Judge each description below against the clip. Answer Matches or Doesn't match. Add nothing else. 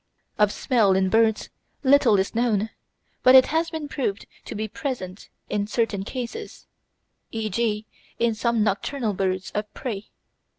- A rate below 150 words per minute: Matches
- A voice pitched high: Matches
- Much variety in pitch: Doesn't match